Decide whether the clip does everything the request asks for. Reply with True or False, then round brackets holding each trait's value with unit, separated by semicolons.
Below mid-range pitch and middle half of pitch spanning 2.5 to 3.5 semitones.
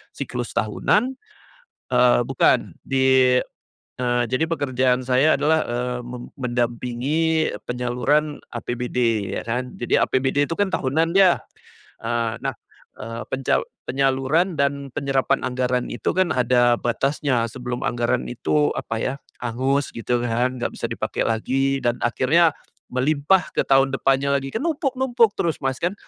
True (130 Hz; 2.8 semitones)